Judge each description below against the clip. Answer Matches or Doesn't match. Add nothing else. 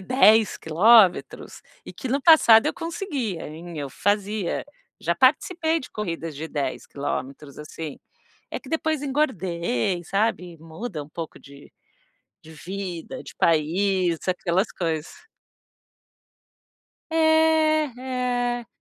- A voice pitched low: Doesn't match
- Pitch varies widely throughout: Matches